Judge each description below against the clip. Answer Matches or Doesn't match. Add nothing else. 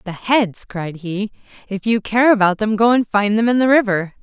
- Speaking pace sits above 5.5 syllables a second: Doesn't match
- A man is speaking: Doesn't match